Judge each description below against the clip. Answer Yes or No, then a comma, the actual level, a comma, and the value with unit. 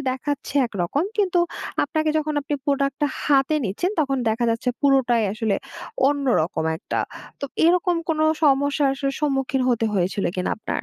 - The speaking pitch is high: Yes, very high, 275 Hz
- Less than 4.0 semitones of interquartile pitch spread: No, average, 4.3 semitones